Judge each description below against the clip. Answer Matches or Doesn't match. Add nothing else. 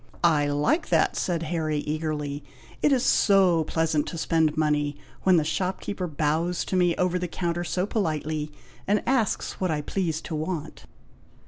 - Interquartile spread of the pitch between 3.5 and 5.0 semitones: Doesn't match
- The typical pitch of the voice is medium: Matches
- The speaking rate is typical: Matches